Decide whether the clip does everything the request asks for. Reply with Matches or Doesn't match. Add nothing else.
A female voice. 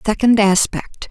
Matches